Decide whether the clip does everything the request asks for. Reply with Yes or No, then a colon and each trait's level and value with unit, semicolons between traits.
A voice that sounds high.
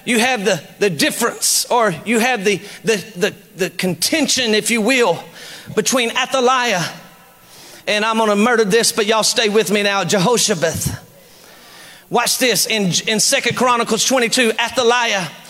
Yes: high, 225 Hz